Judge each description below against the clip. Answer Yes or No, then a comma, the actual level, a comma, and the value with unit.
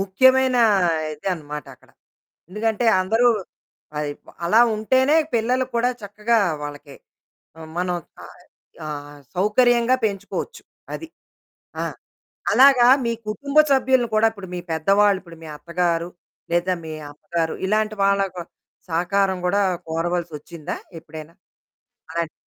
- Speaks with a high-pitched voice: Yes, high, 195 Hz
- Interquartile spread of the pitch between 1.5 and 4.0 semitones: No, wide, 5.6 semitones